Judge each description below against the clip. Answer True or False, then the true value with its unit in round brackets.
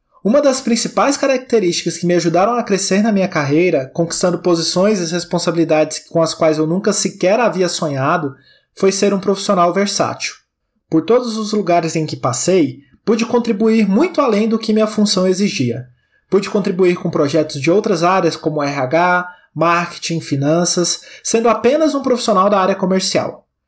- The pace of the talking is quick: False (160 wpm)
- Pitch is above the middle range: False (180 Hz)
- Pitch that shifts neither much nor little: True (4.3 semitones)